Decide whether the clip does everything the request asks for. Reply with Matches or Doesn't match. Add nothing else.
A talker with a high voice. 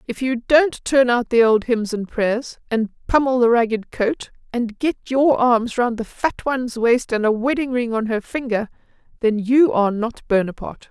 Matches